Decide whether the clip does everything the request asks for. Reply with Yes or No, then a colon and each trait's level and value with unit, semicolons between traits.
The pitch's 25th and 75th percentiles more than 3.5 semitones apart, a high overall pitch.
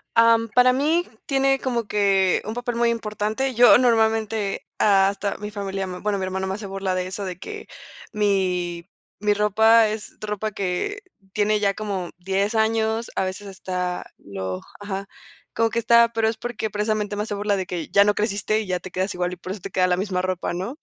No: average, 2.8 semitones; high, 205 Hz